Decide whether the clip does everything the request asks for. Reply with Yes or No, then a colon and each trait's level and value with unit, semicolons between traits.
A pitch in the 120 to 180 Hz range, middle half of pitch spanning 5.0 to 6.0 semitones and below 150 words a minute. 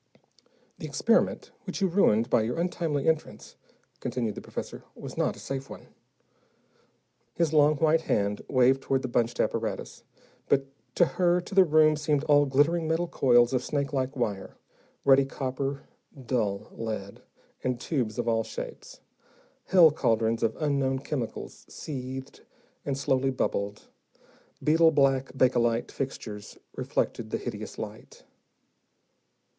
No: low, 135 Hz; average, 4.2 semitones; slow, 135 wpm